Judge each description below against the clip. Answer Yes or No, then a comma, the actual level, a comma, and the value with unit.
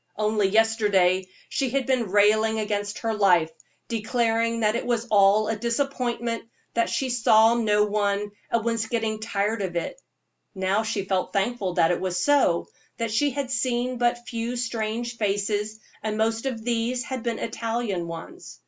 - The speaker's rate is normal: Yes, average, 165 wpm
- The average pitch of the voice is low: No, high, 225 Hz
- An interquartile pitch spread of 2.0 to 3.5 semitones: Yes, narrow, 2.5 semitones